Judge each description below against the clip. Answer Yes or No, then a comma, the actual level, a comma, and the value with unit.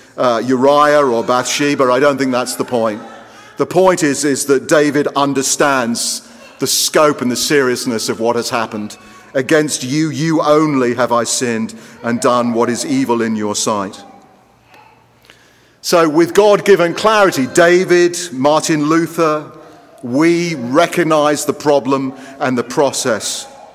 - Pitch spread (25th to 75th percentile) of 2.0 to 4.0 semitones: No, average, 4.5 semitones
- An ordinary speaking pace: Yes, average, 140 wpm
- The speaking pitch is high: No, medium, 140 Hz